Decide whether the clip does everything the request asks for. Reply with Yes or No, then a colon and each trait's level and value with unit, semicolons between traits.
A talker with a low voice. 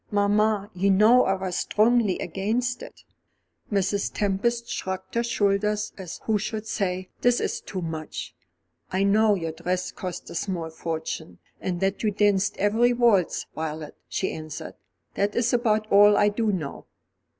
No: high, 200 Hz